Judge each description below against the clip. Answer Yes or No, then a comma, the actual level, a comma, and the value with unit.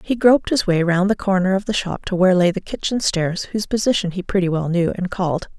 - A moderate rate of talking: No, fast, 260 wpm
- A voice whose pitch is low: No, high, 190 Hz